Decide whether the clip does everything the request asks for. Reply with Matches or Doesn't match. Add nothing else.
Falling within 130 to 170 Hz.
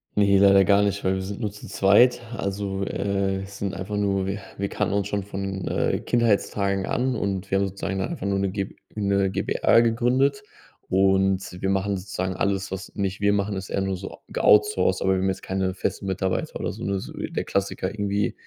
Doesn't match